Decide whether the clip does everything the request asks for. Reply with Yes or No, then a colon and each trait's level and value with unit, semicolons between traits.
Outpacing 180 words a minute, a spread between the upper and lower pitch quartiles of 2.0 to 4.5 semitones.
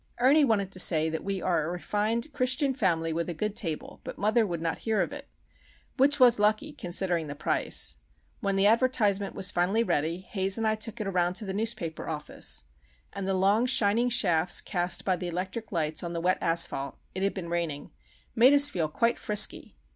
No: average, 195 wpm; average, 4.9 semitones